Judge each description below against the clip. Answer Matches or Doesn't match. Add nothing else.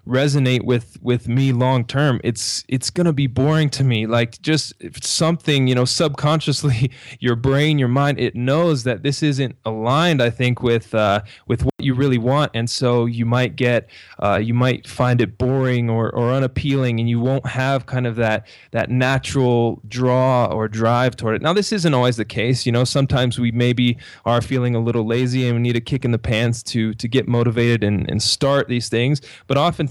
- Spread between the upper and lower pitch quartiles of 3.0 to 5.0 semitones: Doesn't match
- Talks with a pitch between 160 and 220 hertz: Doesn't match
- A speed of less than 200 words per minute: Doesn't match